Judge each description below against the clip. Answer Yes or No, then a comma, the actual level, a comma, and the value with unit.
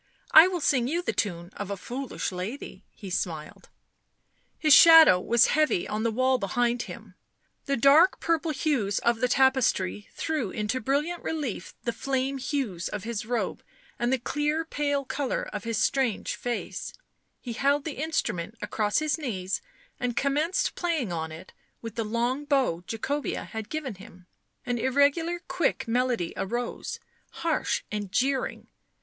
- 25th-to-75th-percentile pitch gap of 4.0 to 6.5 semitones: Yes, wide, 5.5 semitones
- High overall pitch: Yes, very high, 250 Hz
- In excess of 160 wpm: No, average, 155 wpm